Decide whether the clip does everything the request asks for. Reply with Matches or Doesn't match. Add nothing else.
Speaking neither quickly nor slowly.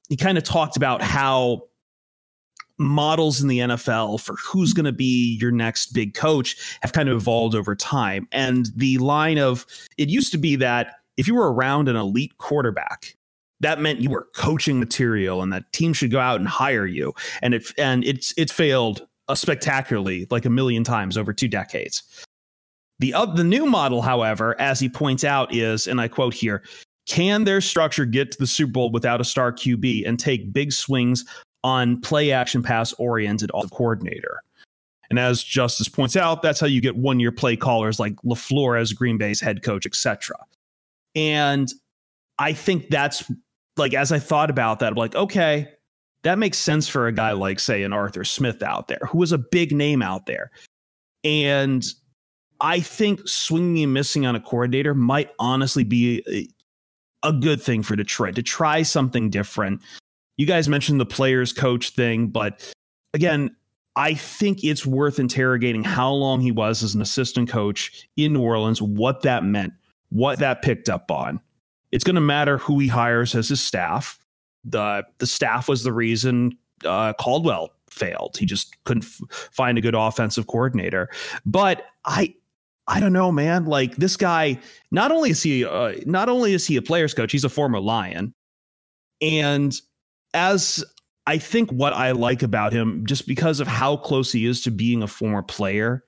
Matches